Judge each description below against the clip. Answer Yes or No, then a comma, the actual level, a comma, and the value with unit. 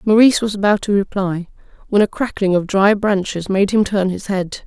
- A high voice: Yes, high, 200 Hz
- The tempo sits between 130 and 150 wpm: No, fast, 205 wpm